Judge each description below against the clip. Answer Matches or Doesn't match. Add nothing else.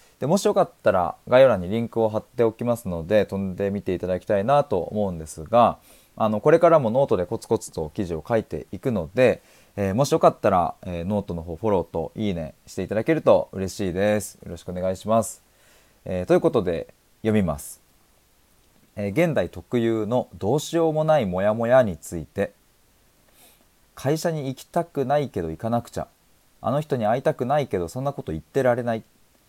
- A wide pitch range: Matches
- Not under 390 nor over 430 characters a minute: Matches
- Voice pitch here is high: Doesn't match